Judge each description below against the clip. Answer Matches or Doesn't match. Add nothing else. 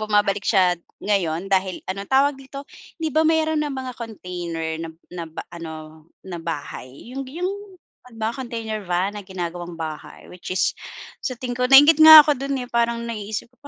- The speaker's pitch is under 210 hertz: Doesn't match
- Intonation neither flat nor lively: Doesn't match